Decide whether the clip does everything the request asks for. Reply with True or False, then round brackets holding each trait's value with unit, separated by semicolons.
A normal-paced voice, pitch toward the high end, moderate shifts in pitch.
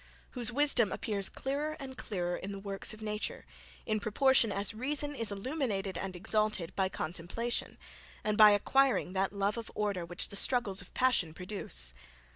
True (165 wpm; 210 Hz; 4.2 semitones)